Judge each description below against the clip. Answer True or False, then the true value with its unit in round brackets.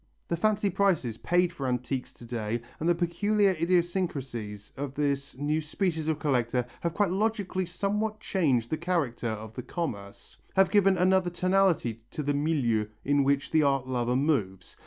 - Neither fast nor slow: True (165 wpm)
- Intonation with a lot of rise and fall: True (6.6 semitones)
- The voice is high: False (155 Hz)